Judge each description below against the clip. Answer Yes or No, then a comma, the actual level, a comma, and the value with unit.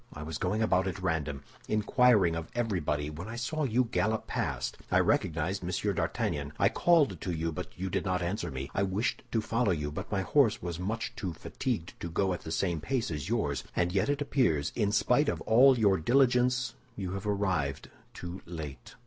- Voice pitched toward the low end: Yes, very low, 95 Hz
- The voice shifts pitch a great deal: Yes, wide, 5.8 semitones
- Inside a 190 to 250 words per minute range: Yes, average, 200 wpm